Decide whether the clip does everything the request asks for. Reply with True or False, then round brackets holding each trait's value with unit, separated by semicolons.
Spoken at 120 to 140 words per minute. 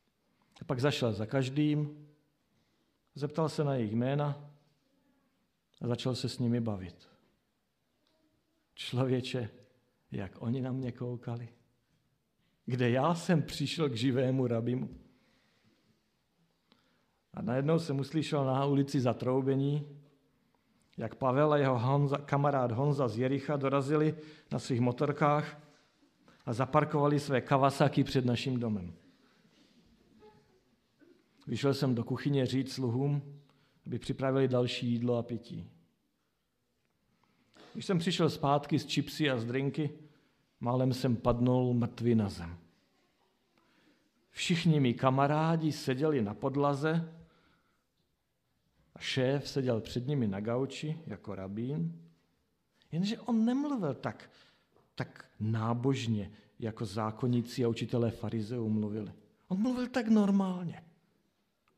False (110 wpm)